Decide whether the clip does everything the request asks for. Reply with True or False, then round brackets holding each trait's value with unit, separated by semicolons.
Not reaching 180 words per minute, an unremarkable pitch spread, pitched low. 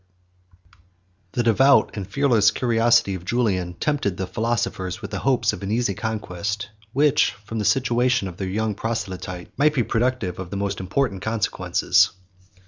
True (160 wpm; 4.2 semitones; 105 Hz)